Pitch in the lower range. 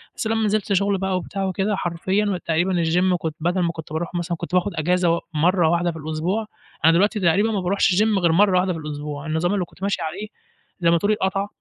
No: medium, 180 Hz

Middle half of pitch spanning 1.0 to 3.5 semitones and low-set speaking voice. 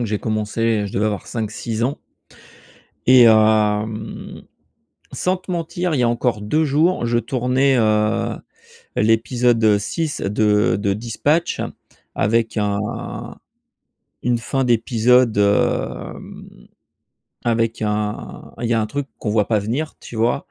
Yes: average, 2.7 semitones; low, 115 Hz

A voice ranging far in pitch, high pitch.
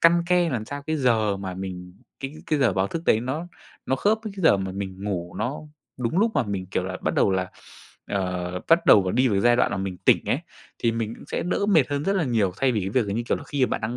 No: wide, 6.9 semitones; low, 115 Hz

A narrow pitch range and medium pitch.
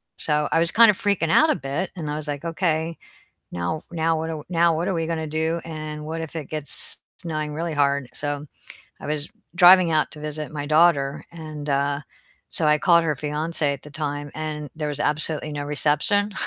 Yes: narrow, 1.9 semitones; medium, 155 Hz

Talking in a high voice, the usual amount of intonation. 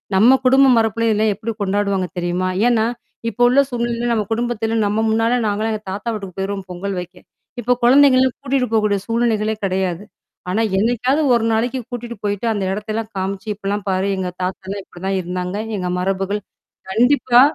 Yes: high, 215 Hz; average, 3.5 semitones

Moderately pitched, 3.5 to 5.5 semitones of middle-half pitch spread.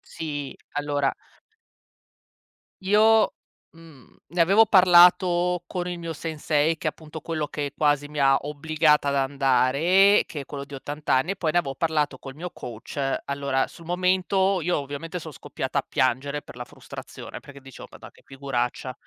Yes: medium, 150 Hz; average, 3.9 semitones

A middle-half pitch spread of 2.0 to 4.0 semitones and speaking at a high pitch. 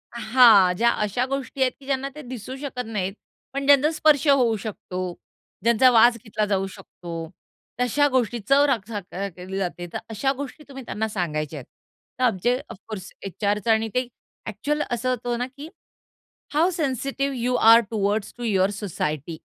No: average, 4.8 semitones; high, 230 Hz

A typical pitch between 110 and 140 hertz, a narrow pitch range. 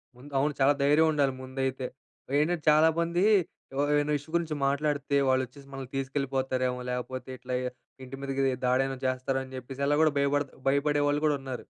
Yes: low, 135 Hz; narrow, 2.0 semitones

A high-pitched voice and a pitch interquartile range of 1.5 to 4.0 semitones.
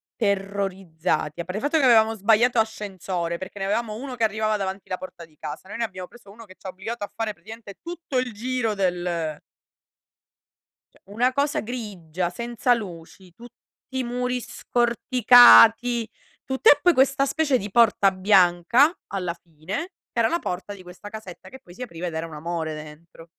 No: high, 205 Hz; average, 5.1 semitones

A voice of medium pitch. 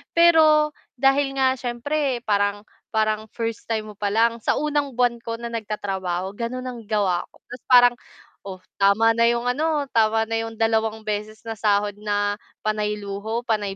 No: high, 225 Hz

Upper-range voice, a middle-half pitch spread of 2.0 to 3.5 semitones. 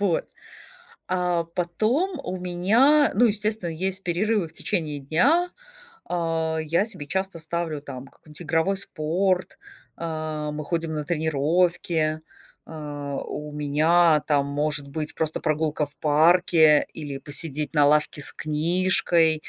No: medium, 160 Hz; average, 3.1 semitones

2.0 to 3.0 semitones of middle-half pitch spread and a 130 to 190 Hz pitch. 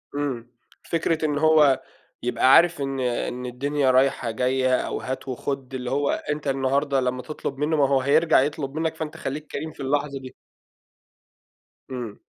Yes: narrow, 2.4 semitones; low, 135 Hz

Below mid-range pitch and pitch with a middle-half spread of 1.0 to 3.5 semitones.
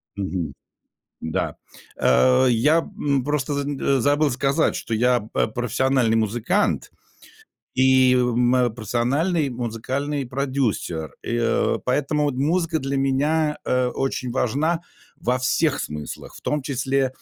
Yes: low, 130 Hz; average, 3.0 semitones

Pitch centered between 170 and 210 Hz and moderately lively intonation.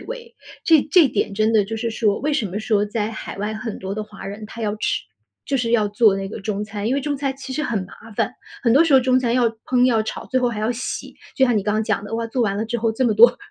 No: high, 225 Hz; average, 3.3 semitones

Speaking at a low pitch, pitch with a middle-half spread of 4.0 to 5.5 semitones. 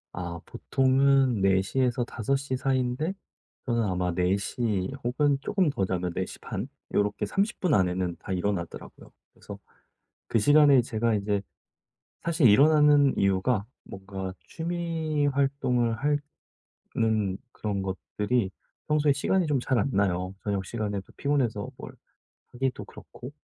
No: low, 120 Hz; wide, 6.3 semitones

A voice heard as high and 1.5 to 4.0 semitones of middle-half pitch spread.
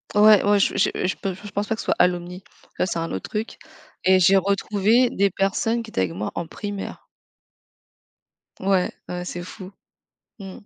Yes: high, 195 Hz; narrow, 2.4 semitones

